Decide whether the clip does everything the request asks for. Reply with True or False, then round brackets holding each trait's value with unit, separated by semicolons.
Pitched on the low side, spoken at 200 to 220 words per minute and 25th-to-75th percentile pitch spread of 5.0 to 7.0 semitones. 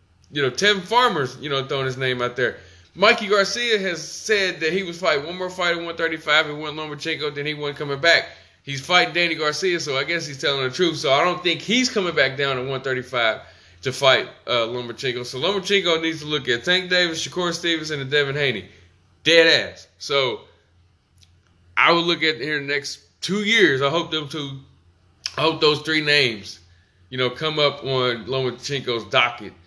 False (150 Hz; 205 wpm; 5.3 semitones)